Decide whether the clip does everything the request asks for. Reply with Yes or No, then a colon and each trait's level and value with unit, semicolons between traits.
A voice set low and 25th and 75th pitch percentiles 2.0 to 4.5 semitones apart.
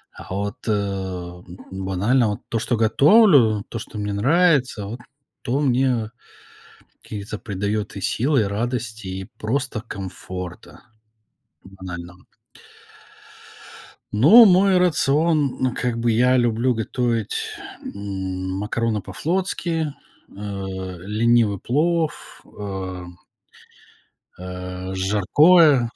No: low, 110 Hz; average, 5.2 semitones